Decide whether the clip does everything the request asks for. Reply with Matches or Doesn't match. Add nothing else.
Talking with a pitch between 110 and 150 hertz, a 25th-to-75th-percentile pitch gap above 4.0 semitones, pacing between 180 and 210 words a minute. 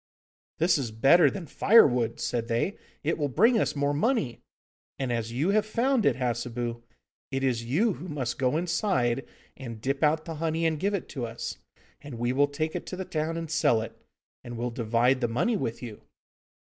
Matches